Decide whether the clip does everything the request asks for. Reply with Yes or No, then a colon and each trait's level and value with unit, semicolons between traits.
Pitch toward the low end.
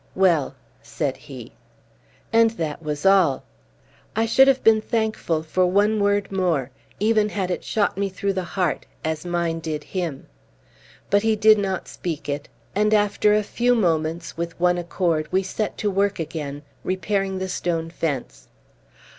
No: medium, 185 Hz